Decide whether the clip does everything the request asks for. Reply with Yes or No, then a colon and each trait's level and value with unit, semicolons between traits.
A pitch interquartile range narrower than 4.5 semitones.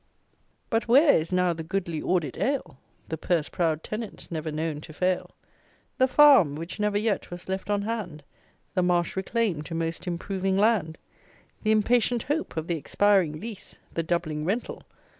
No: average, 4.8 semitones